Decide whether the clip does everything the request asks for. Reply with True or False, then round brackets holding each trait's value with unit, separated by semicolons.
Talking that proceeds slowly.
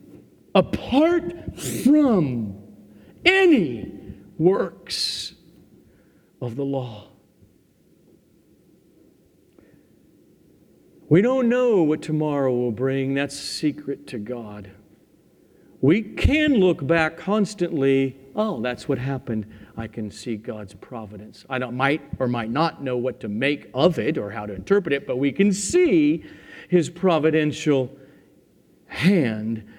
True (115 wpm)